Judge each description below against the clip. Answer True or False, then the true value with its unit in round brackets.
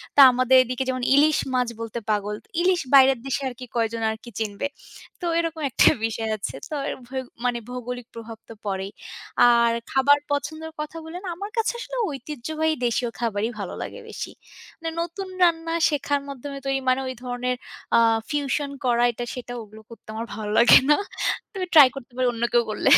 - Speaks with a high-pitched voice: True (255 Hz)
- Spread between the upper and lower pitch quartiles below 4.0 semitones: False (4.3 semitones)